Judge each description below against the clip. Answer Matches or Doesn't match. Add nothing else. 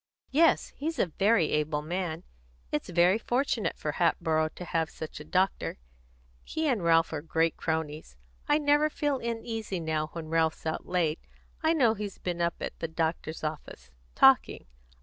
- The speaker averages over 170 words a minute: Doesn't match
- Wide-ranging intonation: Matches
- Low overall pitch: Doesn't match